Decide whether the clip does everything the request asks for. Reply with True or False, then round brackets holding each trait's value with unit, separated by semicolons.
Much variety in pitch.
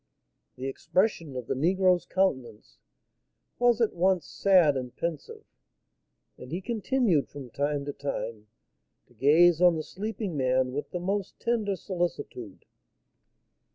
True (6.2 semitones)